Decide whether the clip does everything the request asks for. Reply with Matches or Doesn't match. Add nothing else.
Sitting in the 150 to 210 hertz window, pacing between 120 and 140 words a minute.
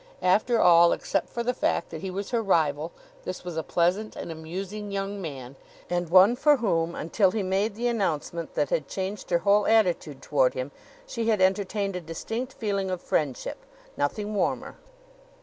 Doesn't match